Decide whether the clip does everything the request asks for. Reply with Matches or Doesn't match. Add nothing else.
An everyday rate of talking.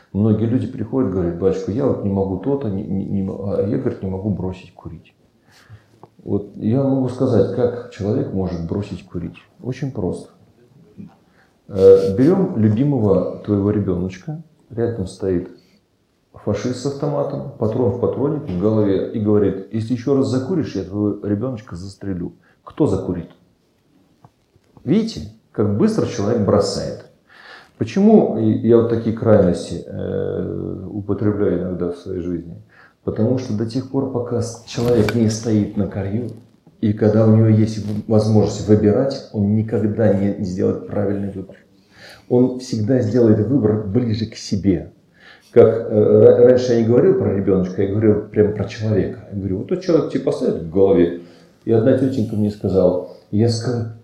Matches